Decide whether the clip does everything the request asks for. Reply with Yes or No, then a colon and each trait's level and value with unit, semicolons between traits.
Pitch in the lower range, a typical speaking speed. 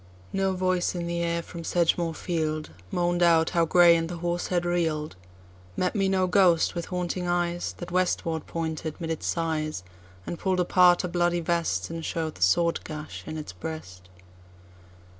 No: medium, 170 Hz; average, 155 wpm